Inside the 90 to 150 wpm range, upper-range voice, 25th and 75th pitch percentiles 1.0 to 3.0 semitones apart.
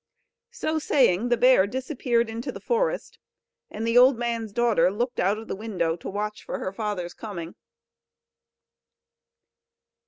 No: average, 145 wpm; high, 225 Hz; average, 3.6 semitones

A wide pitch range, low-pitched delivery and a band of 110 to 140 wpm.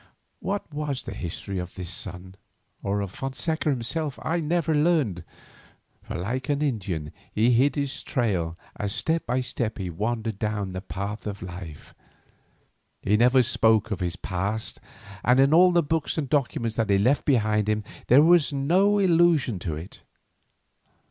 No: wide, 6.9 semitones; low, 115 Hz; average, 160 wpm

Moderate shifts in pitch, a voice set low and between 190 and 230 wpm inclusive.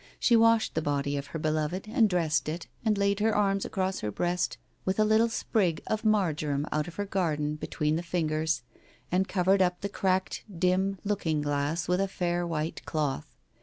No: average, 4.3 semitones; medium, 175 Hz; average, 195 wpm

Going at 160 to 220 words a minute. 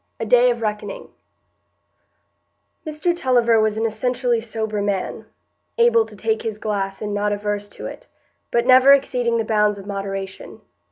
No: average, 150 wpm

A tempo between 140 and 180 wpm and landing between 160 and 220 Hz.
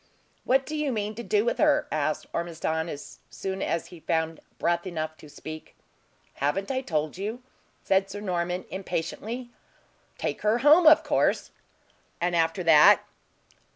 Yes: average, 155 wpm; medium, 185 Hz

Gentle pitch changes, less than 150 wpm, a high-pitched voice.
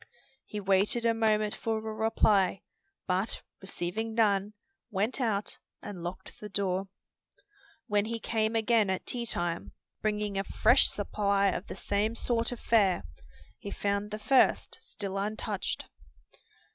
Yes: narrow, 2.1 semitones; average, 140 wpm; high, 210 Hz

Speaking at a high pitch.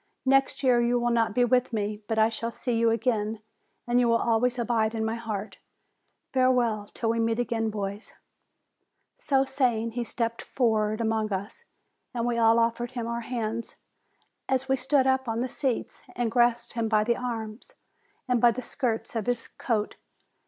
Yes: high, 235 Hz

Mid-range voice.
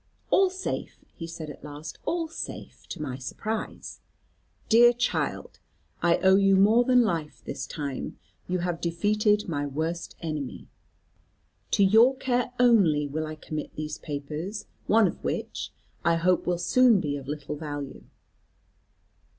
Yes: medium, 170 Hz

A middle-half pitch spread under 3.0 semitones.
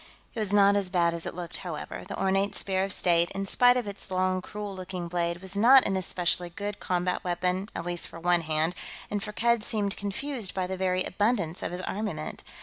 Yes: narrow, 2.4 semitones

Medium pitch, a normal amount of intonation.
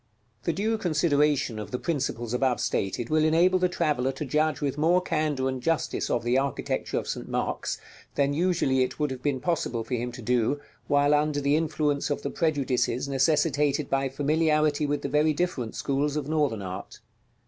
Yes: medium, 145 Hz; average, 3.0 semitones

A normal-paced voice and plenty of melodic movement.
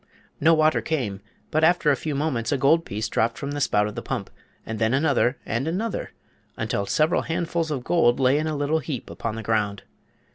No: fast, 210 wpm; wide, 5.7 semitones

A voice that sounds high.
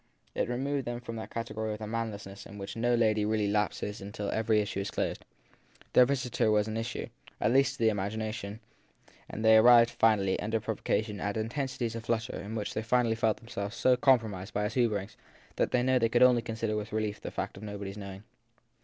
No: low, 110 Hz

